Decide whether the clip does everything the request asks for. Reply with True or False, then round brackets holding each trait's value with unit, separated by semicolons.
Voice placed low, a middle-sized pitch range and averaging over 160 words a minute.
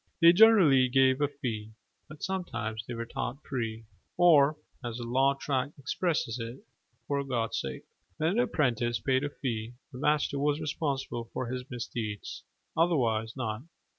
False (130 Hz; 3.9 semitones; 155 wpm)